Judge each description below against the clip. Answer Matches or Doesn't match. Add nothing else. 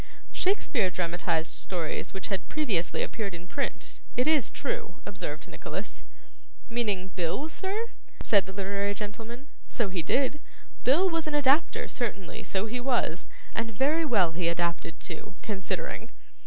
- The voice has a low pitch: Doesn't match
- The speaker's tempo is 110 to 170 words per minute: Matches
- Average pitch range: Doesn't match